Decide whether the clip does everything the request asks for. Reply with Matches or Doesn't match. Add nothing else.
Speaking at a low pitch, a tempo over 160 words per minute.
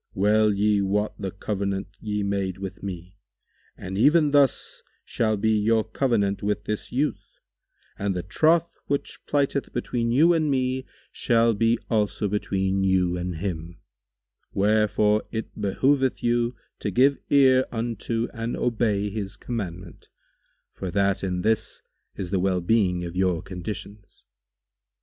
Doesn't match